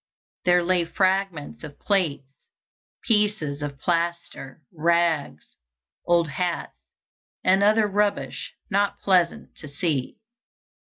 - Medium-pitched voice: Yes, medium, 170 Hz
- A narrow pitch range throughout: No, average, 4.3 semitones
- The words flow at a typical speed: No, slow, 100 wpm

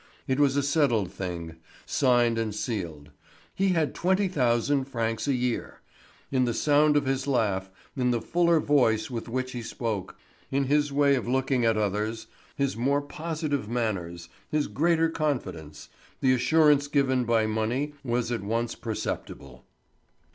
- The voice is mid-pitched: No, low, 125 Hz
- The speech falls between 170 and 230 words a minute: No, average, 155 wpm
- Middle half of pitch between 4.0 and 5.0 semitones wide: Yes, average, 4.4 semitones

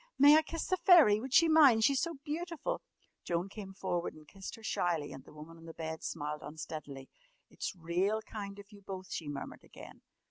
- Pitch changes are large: Yes, wide, 8.6 semitones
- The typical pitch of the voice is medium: No, high, 195 Hz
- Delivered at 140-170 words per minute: No, fast, 205 wpm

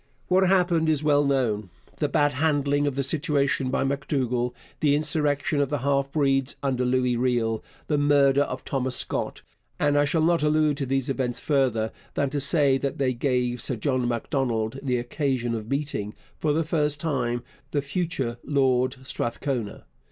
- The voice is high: No, medium, 140 Hz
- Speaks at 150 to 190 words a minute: Yes, average, 170 wpm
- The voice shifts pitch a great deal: No, narrow, 2.6 semitones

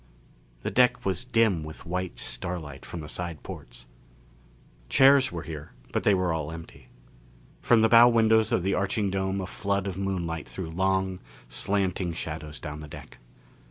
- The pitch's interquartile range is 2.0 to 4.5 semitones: Yes, average, 3.6 semitones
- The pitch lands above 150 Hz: No, very low, 95 Hz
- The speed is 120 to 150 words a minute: No, average, 165 wpm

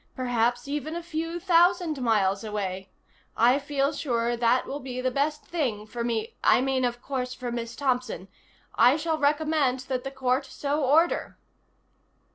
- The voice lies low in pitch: No, very high, 260 Hz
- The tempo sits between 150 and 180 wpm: Yes, average, 160 wpm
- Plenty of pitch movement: No, average, 3.8 semitones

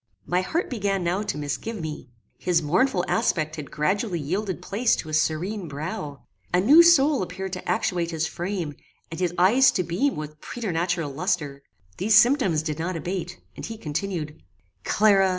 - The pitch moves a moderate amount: Yes, average, 4.6 semitones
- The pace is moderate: Yes, average, 170 wpm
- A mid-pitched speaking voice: Yes, medium, 180 Hz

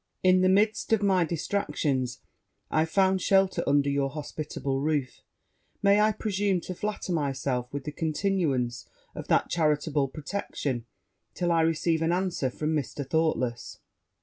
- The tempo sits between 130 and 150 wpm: Yes, average, 145 wpm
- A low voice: No, medium, 160 Hz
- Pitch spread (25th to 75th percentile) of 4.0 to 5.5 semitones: Yes, average, 5.1 semitones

